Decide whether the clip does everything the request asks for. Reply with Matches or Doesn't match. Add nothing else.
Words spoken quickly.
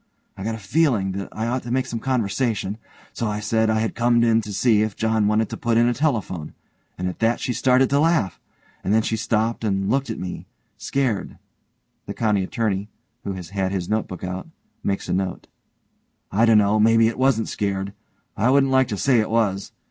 Matches